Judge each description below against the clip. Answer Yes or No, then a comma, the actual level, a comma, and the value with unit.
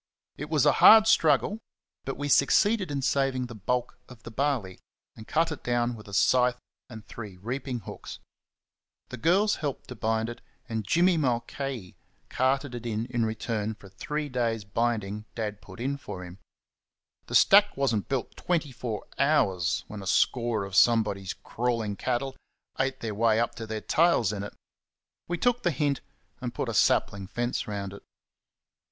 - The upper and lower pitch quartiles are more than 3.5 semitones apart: Yes, average, 4.5 semitones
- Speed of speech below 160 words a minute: No, average, 170 wpm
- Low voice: Yes, low, 120 Hz